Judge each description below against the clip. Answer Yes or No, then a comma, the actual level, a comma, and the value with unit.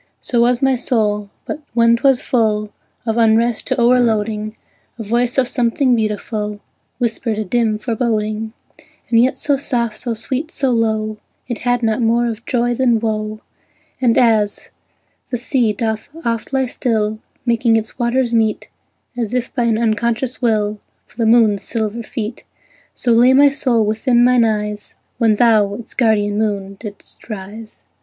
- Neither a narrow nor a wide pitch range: No, narrow, 2.1 semitones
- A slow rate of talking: No, average, 160 wpm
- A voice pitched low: No, high, 230 Hz